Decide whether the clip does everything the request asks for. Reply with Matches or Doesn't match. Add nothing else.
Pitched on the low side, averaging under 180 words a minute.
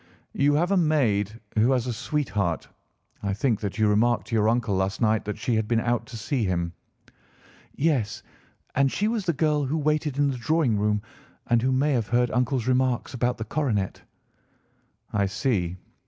Doesn't match